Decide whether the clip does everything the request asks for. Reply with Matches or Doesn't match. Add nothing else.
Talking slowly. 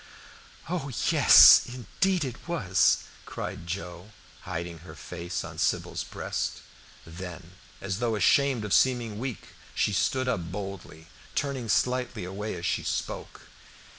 Matches